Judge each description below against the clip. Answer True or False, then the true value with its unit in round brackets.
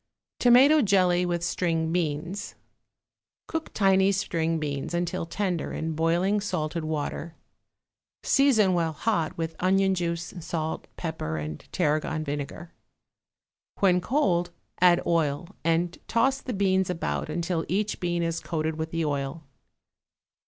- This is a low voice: False (170 Hz)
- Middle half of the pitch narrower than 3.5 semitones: True (2.9 semitones)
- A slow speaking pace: True (125 wpm)